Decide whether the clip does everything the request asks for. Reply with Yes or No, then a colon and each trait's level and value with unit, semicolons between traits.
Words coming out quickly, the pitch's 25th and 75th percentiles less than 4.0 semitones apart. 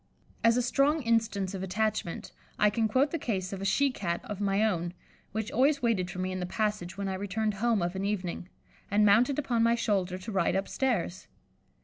Yes: fast, 210 wpm; average, 3.6 semitones